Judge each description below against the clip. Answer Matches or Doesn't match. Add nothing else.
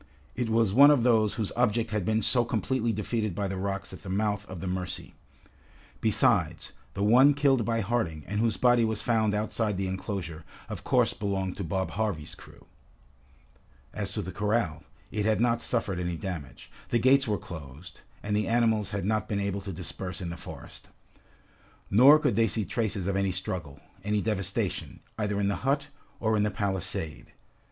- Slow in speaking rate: Doesn't match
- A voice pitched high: Doesn't match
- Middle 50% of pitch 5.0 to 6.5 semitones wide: Doesn't match